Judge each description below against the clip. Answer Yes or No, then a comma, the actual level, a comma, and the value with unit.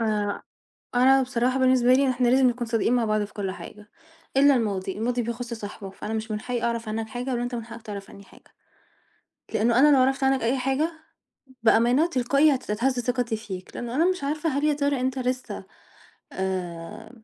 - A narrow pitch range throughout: No, average, 3.3 semitones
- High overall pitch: Yes, high, 245 Hz